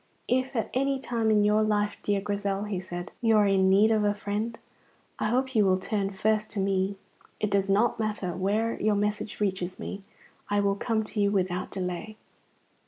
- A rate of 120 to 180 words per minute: No, average, 195 wpm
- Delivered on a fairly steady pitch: Yes, narrow, 1.8 semitones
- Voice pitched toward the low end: No, high, 205 Hz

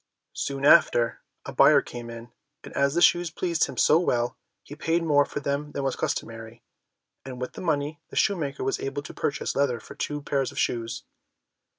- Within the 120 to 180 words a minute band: No, average, 195 wpm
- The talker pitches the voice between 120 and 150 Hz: Yes, medium, 140 Hz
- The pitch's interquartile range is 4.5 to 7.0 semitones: No, average, 3.4 semitones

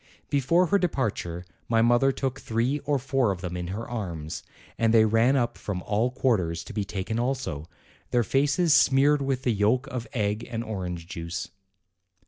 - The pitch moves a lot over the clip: Yes, wide, 5.7 semitones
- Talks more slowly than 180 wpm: Yes, average, 170 wpm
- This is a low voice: Yes, low, 115 Hz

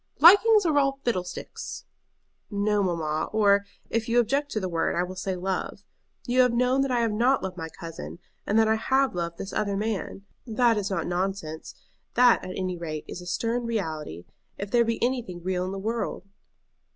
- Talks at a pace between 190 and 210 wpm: Yes, average, 195 wpm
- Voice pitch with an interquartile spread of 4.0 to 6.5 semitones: Yes, average, 4.8 semitones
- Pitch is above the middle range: Yes, high, 205 Hz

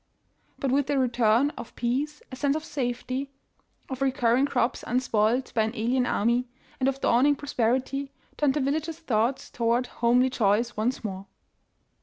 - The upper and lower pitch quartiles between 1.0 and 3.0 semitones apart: Yes, average, 2.7 semitones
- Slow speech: No, average, 160 wpm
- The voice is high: Yes, very high, 255 Hz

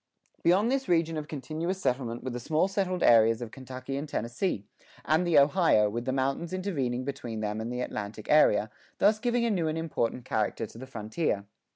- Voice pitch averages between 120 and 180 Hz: Yes, low, 135 Hz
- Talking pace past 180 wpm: Yes, average, 200 wpm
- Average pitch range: No, wide, 6.5 semitones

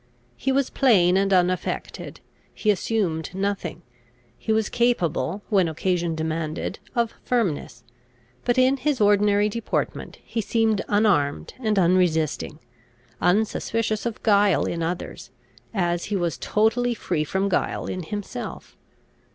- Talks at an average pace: No, slow, 125 wpm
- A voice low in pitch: No, high, 200 Hz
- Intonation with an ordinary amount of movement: Yes, average, 4.3 semitones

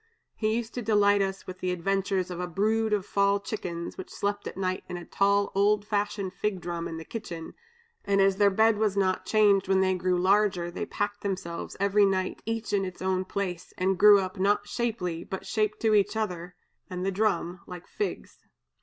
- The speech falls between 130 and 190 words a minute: No, fast, 205 wpm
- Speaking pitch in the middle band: No, high, 195 Hz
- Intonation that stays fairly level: Yes, narrow, 2.1 semitones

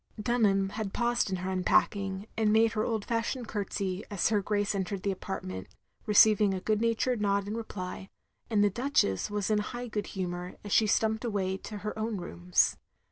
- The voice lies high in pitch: Yes, high, 205 Hz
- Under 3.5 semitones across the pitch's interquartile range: Yes, narrow, 2.4 semitones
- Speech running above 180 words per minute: Yes, average, 190 wpm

